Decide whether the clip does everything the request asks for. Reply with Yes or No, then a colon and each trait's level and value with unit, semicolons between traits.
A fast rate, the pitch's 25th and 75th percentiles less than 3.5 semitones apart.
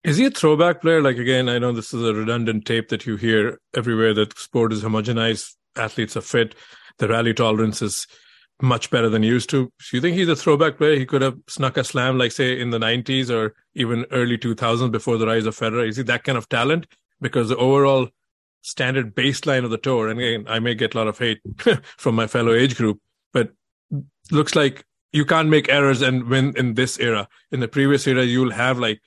Yes: fast, 225 wpm; average, 3.0 semitones